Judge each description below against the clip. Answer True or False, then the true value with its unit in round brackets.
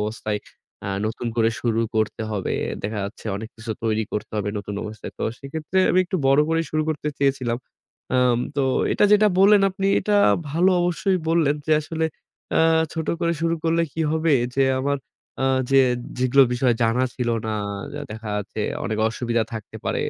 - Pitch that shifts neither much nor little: False (6.5 semitones)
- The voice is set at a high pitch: False (135 Hz)